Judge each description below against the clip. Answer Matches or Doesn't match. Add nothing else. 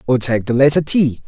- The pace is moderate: Doesn't match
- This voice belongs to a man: Matches